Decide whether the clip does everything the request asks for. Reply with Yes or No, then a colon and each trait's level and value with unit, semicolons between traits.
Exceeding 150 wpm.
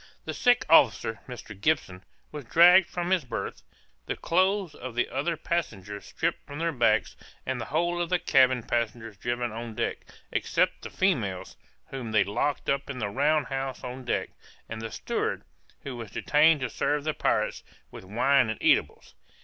Yes: average, 175 wpm